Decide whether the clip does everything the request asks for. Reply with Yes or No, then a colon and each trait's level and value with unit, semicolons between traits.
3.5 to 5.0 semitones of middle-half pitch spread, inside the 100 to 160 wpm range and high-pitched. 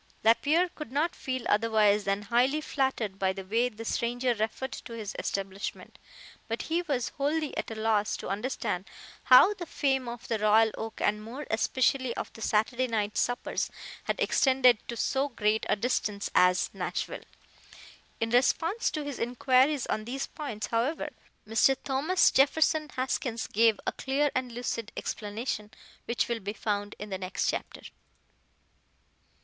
Yes: average, 4.0 semitones; average, 155 wpm; high, 235 Hz